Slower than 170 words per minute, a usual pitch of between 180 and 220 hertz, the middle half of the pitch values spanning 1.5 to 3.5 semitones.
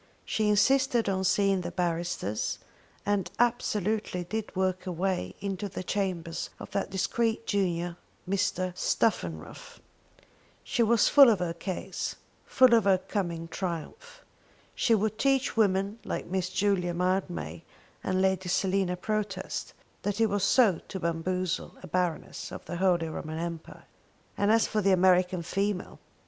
Yes: average, 140 wpm; high, 190 Hz; average, 2.8 semitones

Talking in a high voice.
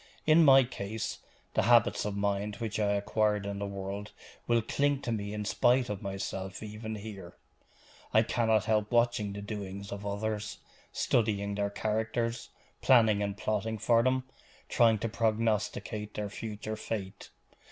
No: low, 105 Hz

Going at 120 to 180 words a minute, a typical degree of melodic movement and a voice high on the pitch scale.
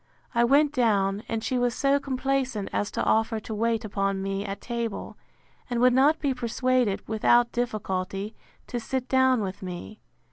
Yes: average, 170 wpm; average, 3.9 semitones; high, 235 Hz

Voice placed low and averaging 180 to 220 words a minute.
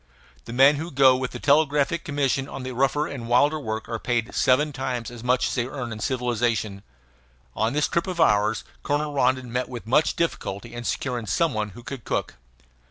Yes: low, 130 Hz; average, 200 wpm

